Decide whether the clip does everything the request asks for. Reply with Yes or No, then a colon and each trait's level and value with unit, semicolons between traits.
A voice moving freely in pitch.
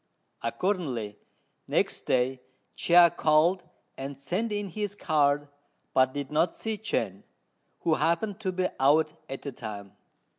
Yes: wide, 5.7 semitones